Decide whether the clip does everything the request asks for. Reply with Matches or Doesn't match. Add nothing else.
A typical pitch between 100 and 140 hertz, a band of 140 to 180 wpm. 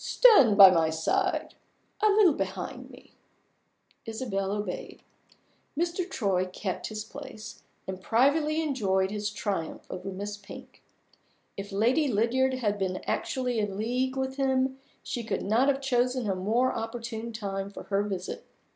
Doesn't match